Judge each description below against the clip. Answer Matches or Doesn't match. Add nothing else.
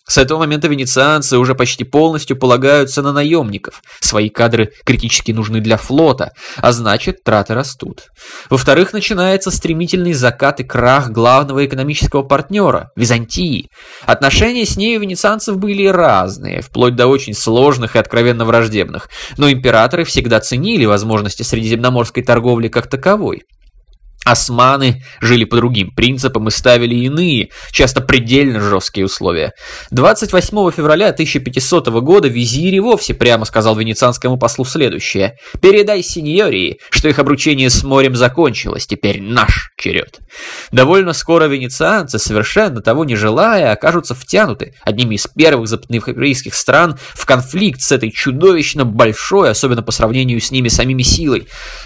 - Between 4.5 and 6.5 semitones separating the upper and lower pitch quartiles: Matches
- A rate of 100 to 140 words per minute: Matches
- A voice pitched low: Matches